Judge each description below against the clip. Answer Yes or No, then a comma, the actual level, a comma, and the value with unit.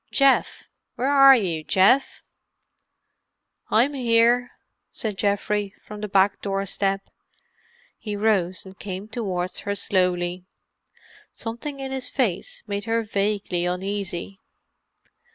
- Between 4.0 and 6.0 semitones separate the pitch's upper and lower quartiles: No, average, 3.3 semitones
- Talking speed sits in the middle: No, slow, 110 wpm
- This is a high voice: Yes, high, 205 Hz